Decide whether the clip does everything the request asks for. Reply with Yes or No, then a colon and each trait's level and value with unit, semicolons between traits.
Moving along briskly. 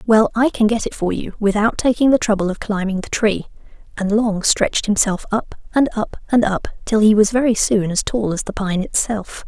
Yes: fast, 220 wpm